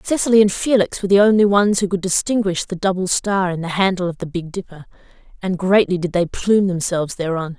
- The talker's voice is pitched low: No, medium, 185 Hz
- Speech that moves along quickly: Yes, fast, 215 wpm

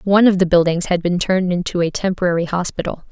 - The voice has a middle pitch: Yes, medium, 180 Hz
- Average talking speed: No, fast, 210 wpm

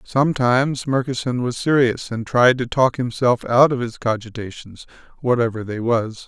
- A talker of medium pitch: No, low, 125 Hz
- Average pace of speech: Yes, average, 155 wpm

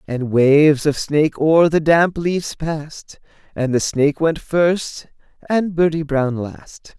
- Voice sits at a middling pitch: Yes, medium, 150 Hz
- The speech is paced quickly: No, average, 155 wpm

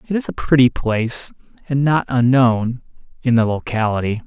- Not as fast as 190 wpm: Yes, average, 140 wpm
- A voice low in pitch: Yes, low, 125 Hz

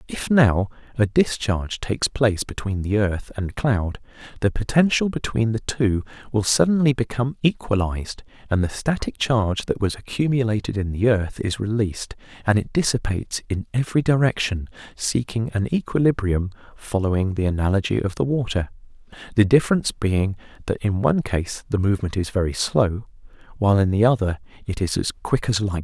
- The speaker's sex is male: Yes, male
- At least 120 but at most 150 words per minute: No, average, 160 wpm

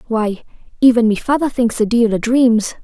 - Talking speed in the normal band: Yes, average, 190 wpm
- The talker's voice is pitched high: Yes, high, 230 Hz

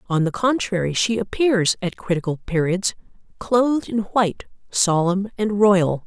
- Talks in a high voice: Yes, high, 195 Hz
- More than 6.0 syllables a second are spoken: No, 4.5 syllables/s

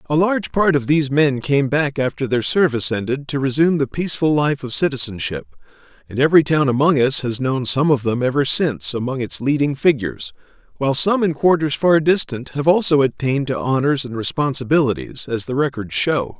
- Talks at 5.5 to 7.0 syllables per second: Yes, 5.7 syllables/s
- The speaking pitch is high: No, low, 135 Hz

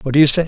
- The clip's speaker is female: No, male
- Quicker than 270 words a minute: Yes, fast, 510 wpm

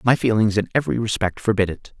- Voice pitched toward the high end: No, low, 105 Hz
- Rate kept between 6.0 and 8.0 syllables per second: Yes, 6.6 syllables/s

